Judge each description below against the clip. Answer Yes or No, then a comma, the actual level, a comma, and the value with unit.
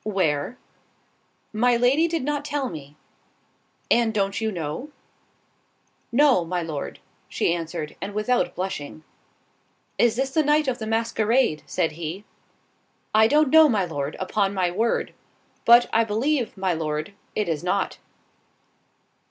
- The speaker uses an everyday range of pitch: No, wide, 6.6 semitones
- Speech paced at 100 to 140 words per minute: Yes, slow, 135 wpm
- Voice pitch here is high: Yes, high, 215 Hz